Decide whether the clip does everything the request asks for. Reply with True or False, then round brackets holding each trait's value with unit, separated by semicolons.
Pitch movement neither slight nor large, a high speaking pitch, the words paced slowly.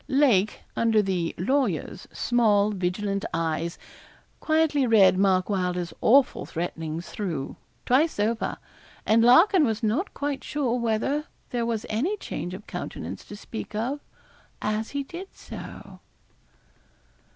False (6.3 semitones; 220 Hz; 125 wpm)